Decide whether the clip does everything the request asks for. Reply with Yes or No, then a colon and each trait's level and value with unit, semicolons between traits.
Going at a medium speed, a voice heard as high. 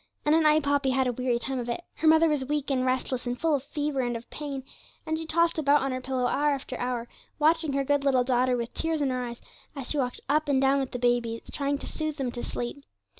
No: fast, 265 wpm; very high, 270 Hz